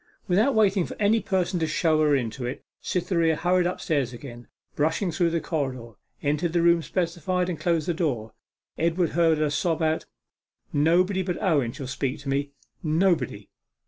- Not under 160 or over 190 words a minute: Yes, average, 170 wpm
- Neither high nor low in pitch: Yes, medium, 165 Hz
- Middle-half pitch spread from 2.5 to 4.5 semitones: Yes, average, 3.8 semitones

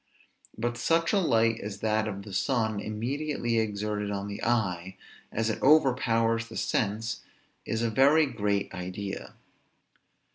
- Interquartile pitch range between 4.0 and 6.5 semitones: No, average, 2.7 semitones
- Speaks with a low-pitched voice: Yes, low, 110 Hz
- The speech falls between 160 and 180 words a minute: No, average, 140 wpm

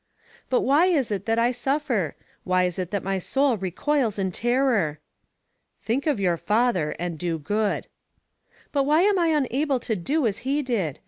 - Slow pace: No, average, 180 wpm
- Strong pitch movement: Yes, wide, 6.9 semitones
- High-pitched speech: Yes, high, 230 Hz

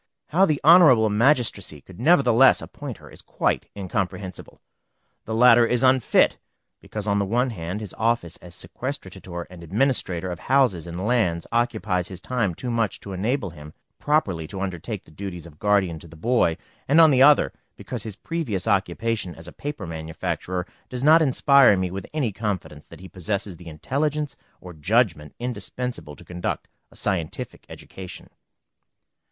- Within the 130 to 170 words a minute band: Yes, average, 165 wpm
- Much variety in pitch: Yes, wide, 6.0 semitones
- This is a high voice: No, low, 100 Hz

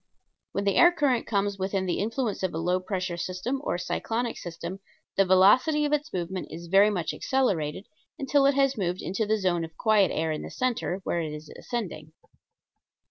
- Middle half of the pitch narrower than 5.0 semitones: No, wide, 5.6 semitones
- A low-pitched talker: No, high, 195 Hz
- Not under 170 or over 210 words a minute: Yes, average, 190 wpm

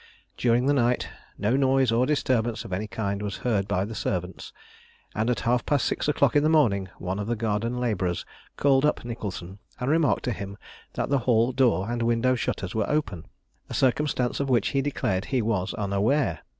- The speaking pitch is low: Yes, low, 115 Hz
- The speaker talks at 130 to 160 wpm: No, average, 195 wpm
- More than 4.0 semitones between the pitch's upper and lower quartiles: Yes, average, 4.5 semitones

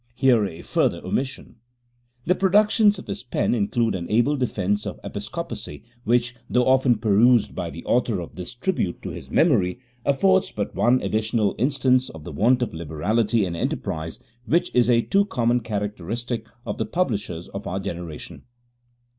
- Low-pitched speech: Yes, low, 115 Hz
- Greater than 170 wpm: No, average, 165 wpm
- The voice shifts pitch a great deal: No, average, 4.5 semitones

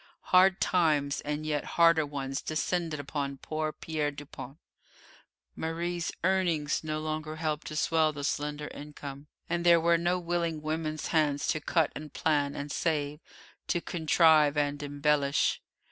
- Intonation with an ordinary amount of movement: No, narrow, 2.1 semitones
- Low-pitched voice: No, medium, 155 Hz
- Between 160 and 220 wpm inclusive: No, average, 145 wpm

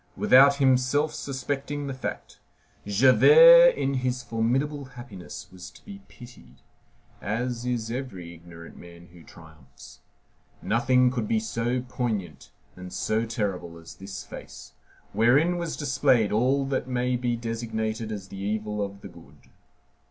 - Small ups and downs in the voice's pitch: No, average, 4.6 semitones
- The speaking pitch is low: Yes, low, 120 Hz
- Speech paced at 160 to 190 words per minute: No, slow, 135 wpm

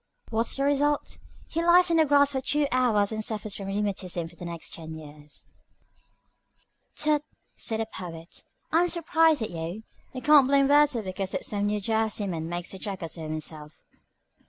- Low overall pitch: No, high, 215 Hz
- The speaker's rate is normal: Yes, average, 175 wpm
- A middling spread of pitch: No, wide, 8.5 semitones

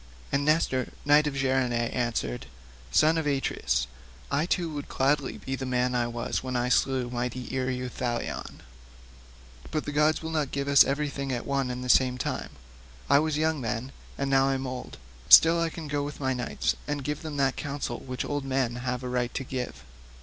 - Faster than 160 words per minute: Yes, average, 195 wpm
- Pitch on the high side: No, low, 135 Hz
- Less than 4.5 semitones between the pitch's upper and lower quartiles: Yes, narrow, 2.6 semitones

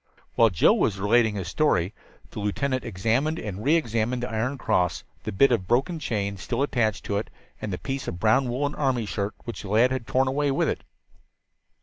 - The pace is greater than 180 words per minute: Yes, fast, 205 wpm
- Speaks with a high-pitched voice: No, low, 115 Hz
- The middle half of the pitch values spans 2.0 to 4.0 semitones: No, average, 4.5 semitones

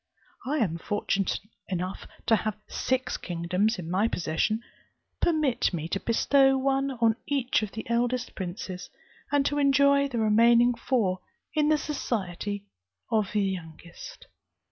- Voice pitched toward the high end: Yes, high, 225 Hz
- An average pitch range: No, wide, 5.9 semitones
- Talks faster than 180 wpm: No, average, 140 wpm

